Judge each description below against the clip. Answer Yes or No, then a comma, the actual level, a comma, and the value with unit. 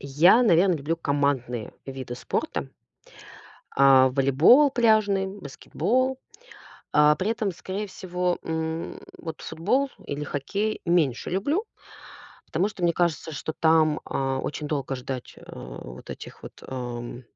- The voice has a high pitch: No, medium, 160 Hz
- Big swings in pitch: Yes, wide, 6.1 semitones